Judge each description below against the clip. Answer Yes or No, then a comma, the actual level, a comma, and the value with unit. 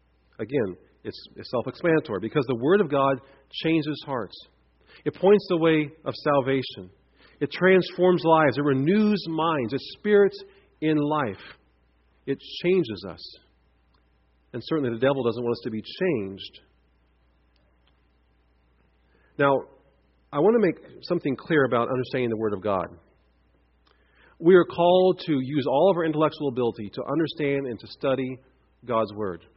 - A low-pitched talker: Yes, low, 130 Hz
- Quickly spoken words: No, average, 140 wpm